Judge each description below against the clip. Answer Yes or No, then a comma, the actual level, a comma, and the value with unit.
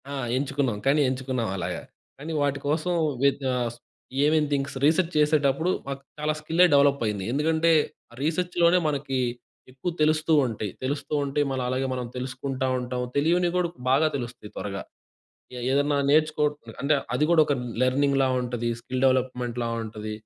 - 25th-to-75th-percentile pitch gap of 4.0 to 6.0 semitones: No, average, 3.2 semitones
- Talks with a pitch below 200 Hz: Yes, medium, 140 Hz